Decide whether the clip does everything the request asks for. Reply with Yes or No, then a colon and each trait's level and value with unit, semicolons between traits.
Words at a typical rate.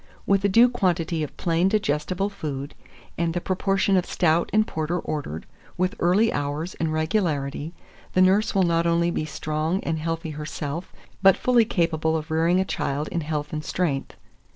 Yes: average, 175 wpm